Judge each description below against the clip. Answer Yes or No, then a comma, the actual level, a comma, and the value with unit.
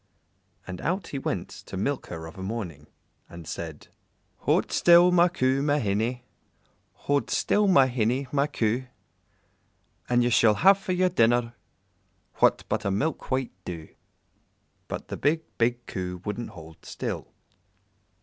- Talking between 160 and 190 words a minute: No, average, 150 wpm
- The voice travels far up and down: Yes, wide, 6.8 semitones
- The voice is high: No, low, 120 Hz